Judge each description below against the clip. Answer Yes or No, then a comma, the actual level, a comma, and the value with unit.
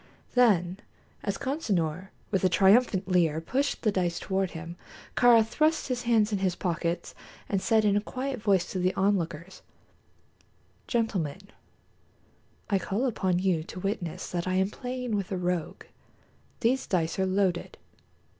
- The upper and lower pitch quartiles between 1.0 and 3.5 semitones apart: No, average, 3.9 semitones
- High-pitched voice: Yes, high, 195 Hz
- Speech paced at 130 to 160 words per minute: Yes, average, 150 wpm